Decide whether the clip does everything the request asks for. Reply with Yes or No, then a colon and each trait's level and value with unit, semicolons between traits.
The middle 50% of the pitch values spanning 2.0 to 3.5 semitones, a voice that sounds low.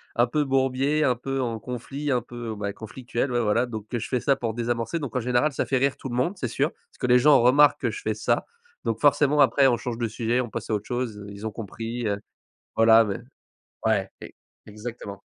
Yes: average, 2.9 semitones; low, 120 Hz